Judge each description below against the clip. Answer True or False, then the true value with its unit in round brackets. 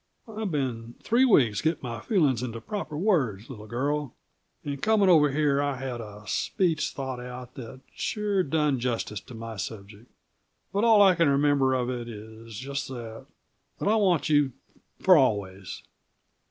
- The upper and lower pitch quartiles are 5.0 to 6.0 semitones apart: True (5.6 semitones)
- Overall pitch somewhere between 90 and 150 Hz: True (135 Hz)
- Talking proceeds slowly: False (165 wpm)